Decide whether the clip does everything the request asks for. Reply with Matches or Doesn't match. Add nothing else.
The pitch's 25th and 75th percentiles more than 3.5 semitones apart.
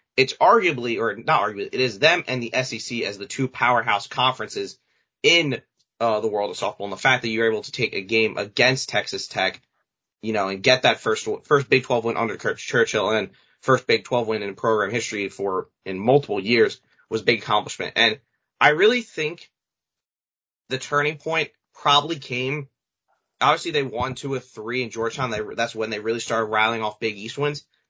Matches